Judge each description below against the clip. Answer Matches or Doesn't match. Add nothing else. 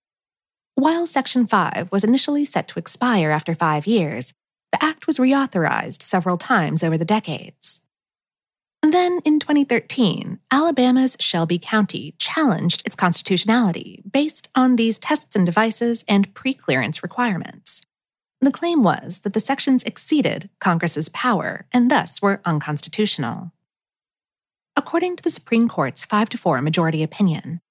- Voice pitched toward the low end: Doesn't match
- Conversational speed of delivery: Doesn't match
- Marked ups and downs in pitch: Matches